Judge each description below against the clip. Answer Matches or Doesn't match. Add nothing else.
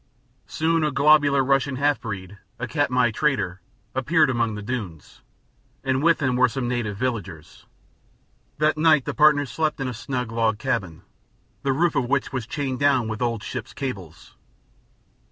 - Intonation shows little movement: Doesn't match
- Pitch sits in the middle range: Doesn't match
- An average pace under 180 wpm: Matches